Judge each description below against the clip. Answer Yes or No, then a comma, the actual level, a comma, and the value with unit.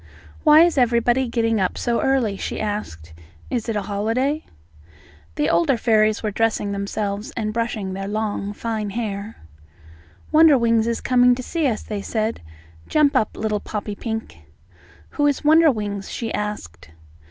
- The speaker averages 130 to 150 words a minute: Yes, average, 145 wpm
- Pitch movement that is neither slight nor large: Yes, average, 3.1 semitones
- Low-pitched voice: No, high, 220 Hz